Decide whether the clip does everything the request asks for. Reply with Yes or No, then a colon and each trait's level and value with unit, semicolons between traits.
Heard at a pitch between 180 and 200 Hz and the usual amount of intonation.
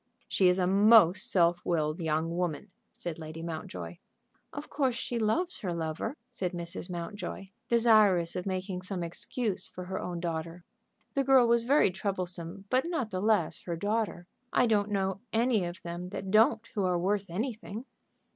Yes: high, 190 Hz; average, 4.2 semitones